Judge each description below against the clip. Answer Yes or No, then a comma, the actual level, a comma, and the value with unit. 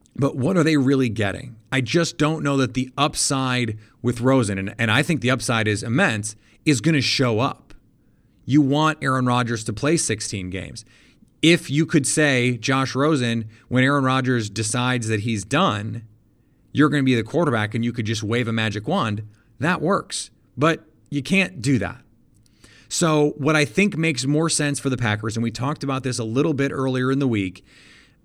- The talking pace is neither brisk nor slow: Yes, average, 195 wpm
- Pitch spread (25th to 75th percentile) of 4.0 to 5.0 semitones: Yes, average, 4.3 semitones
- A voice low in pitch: Yes, low, 130 Hz